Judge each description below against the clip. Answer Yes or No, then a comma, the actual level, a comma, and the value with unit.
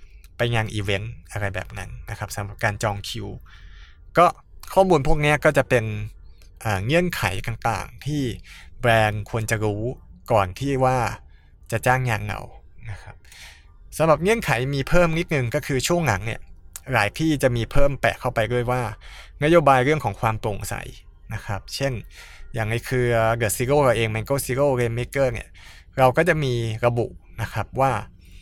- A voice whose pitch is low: Yes, low, 115 Hz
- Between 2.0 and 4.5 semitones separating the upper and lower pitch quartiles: No, average, 4.9 semitones